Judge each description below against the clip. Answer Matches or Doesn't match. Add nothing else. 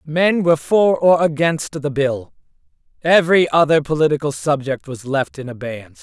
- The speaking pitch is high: Doesn't match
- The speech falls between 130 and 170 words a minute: Matches